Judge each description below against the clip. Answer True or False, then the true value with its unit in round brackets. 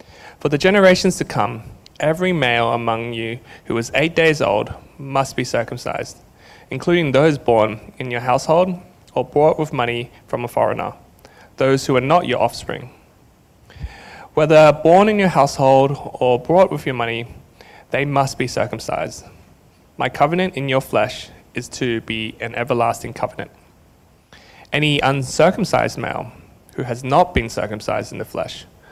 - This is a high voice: False (135 Hz)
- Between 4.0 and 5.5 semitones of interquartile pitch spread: True (4.6 semitones)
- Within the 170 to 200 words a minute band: False (150 wpm)